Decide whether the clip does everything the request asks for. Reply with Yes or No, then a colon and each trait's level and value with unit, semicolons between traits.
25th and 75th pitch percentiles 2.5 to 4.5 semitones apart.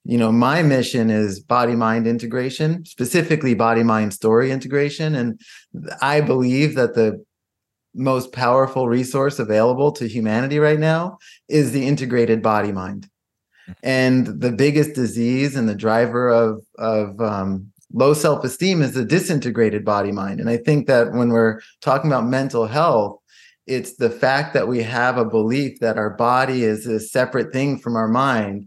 Yes: average, 3.2 semitones